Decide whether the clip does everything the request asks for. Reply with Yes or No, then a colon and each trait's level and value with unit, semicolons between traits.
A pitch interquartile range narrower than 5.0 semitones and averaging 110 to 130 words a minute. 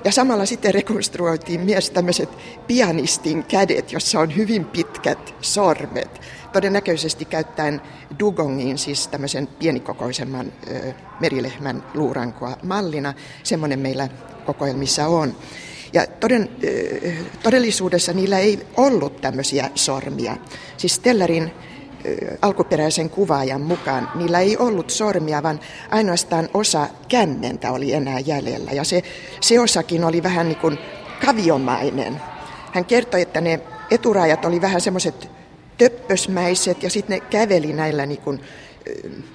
No: average, 5.3 semitones; average, 115 wpm